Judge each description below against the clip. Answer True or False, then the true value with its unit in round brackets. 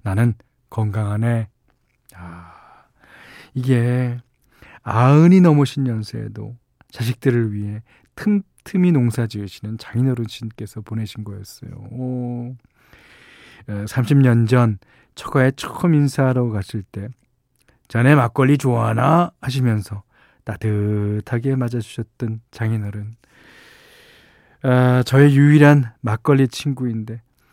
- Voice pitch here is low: True (120 Hz)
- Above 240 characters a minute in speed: False (225 characters per minute)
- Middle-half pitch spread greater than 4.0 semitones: False (3.1 semitones)